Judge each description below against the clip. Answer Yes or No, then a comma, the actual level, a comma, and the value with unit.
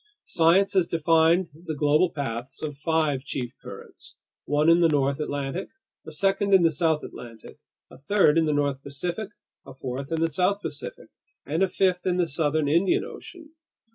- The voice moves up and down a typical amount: Yes, average, 3.9 semitones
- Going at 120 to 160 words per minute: No, average, 175 wpm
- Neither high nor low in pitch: Yes, medium, 160 Hz